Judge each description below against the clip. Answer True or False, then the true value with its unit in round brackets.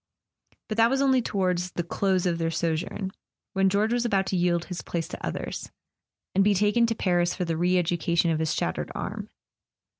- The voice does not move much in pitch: False (3.1 semitones)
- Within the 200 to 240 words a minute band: True (205 wpm)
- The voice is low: False (180 Hz)